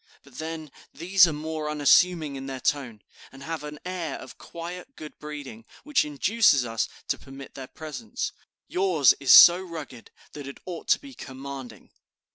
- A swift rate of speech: No, average, 165 wpm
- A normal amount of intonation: Yes, average, 3.9 semitones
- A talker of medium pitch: Yes, medium, 150 Hz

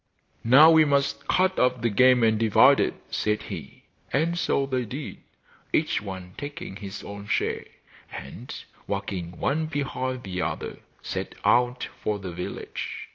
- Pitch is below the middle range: Yes, low, 125 Hz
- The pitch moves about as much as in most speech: No, wide, 5.7 semitones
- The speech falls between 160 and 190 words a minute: No, average, 150 wpm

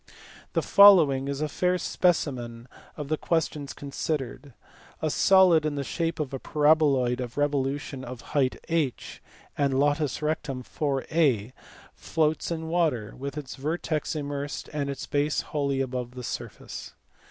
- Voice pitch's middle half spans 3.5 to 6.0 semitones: No, average, 2.8 semitones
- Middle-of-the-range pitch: Yes, medium, 145 Hz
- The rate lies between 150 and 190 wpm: No, average, 140 wpm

